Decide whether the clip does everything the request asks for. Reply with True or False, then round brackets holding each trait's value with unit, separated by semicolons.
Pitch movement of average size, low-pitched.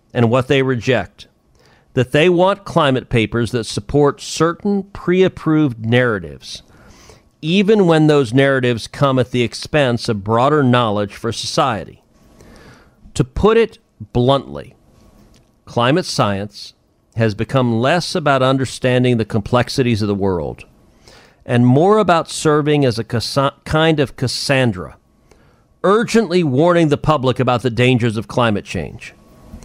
True (4.6 semitones; 130 Hz)